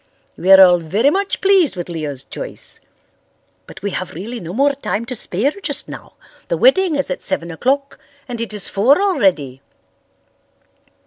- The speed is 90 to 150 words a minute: No, average, 170 wpm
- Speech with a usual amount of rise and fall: No, wide, 8.1 semitones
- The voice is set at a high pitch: Yes, high, 220 Hz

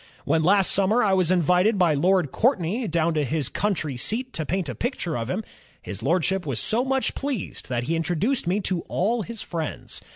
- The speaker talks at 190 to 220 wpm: Yes, average, 200 wpm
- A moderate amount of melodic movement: Yes, average, 5.0 semitones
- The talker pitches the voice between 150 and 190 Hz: Yes, medium, 185 Hz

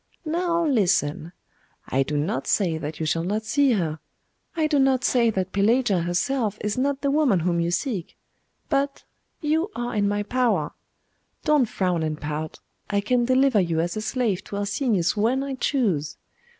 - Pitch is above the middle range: Yes, high, 215 Hz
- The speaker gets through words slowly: No, average, 175 wpm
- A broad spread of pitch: Yes, wide, 7.4 semitones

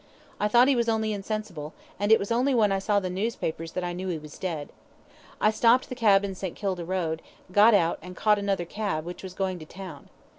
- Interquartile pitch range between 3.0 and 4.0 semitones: Yes, average, 3.5 semitones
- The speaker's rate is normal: No, fast, 230 wpm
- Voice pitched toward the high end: Yes, high, 195 Hz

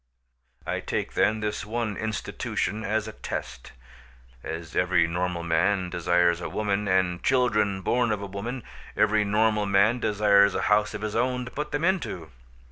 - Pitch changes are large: No, average, 3.3 semitones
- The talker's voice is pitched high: No, low, 105 Hz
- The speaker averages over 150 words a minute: Yes, average, 165 wpm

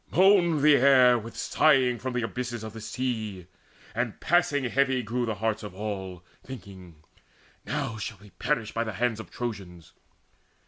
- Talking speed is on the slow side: No, average, 165 wpm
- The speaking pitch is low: Yes, low, 115 Hz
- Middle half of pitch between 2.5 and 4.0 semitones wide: Yes, average, 3.7 semitones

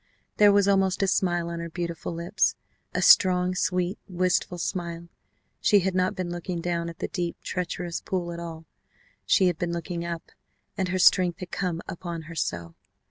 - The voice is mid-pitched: Yes, medium, 175 Hz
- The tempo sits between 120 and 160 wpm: No, average, 185 wpm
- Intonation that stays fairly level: Yes, narrow, 1.4 semitones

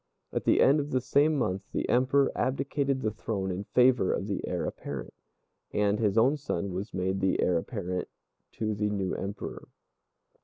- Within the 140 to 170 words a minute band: No, average, 180 wpm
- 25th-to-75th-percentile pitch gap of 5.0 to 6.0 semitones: Yes, average, 5.3 semitones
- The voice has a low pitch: Yes, low, 105 Hz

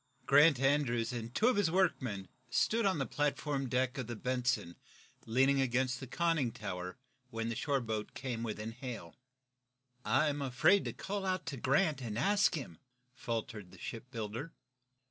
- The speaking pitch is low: Yes, low, 130 Hz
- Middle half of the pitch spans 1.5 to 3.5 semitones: No, average, 4.3 semitones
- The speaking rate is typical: Yes, average, 165 wpm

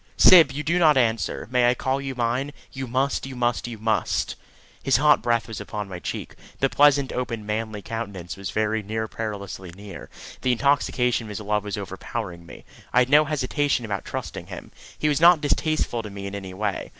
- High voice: No, low, 115 Hz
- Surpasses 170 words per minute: Yes, average, 200 wpm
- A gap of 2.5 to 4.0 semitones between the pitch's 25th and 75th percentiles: No, average, 4.6 semitones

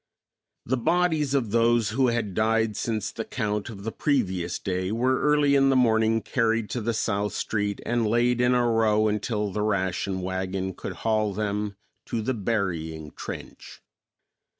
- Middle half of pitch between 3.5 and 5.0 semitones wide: No, average, 2.9 semitones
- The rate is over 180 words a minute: No, average, 165 wpm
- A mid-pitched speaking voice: No, low, 110 Hz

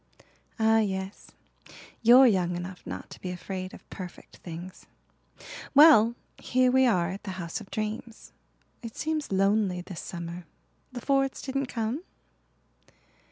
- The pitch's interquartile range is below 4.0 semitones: No, average, 5.2 semitones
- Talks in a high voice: Yes, high, 210 Hz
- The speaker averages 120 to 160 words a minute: Yes, slow, 135 wpm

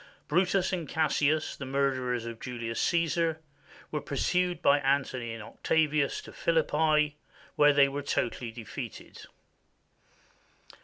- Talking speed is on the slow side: Yes, slow, 115 wpm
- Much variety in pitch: No, average, 3.7 semitones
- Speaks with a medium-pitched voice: Yes, medium, 145 Hz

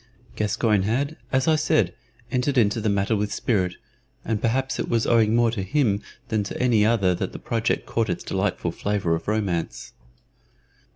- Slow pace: No, average, 175 wpm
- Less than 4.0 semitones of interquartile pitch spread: Yes, average, 2.8 semitones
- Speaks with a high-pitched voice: No, low, 110 Hz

